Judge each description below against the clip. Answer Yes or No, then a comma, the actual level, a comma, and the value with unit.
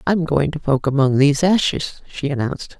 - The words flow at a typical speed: Yes, average, 195 wpm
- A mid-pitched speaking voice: Yes, medium, 150 Hz